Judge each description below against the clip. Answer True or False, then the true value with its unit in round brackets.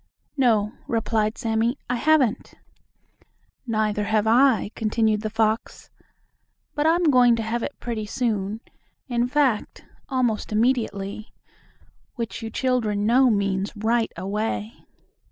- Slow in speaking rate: True (120 wpm)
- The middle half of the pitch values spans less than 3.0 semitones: True (2.5 semitones)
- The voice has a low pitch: False (225 Hz)